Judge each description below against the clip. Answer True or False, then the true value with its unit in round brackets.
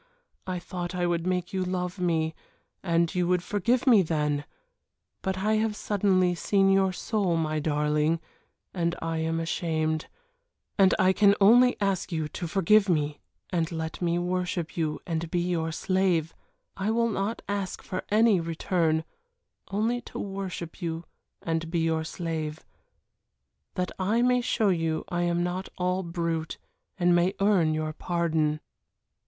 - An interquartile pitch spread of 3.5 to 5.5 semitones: False (2.9 semitones)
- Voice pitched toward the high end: False (175 Hz)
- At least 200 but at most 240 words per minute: False (155 wpm)